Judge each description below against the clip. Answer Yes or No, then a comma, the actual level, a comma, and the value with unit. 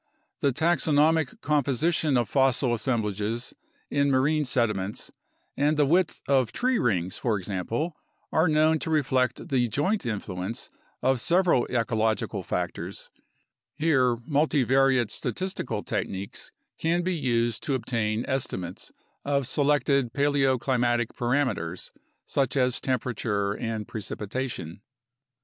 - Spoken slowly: Yes, slow, 115 wpm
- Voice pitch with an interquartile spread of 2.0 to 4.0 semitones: No, average, 4.5 semitones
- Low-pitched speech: Yes, low, 130 Hz